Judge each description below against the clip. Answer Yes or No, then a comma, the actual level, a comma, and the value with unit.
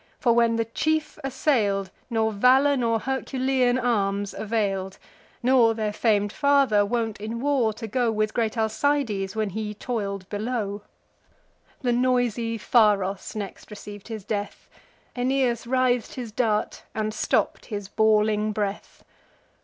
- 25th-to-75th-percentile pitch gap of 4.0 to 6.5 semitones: No, average, 3.0 semitones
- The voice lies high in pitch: Yes, high, 225 Hz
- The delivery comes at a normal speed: No, slow, 130 wpm